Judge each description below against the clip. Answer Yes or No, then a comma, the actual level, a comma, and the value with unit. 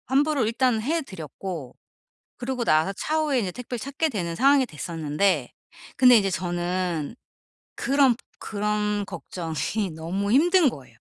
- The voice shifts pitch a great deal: Yes, wide, 7.1 semitones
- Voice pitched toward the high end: Yes, high, 210 Hz